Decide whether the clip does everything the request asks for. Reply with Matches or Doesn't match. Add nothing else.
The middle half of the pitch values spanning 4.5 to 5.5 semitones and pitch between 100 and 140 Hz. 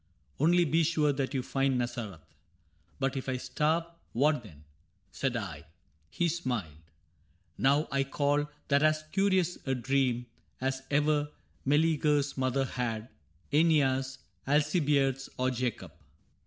Doesn't match